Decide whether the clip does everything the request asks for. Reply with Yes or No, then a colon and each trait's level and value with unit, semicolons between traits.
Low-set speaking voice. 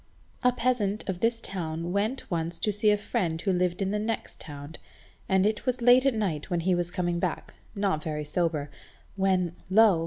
No: high, 190 Hz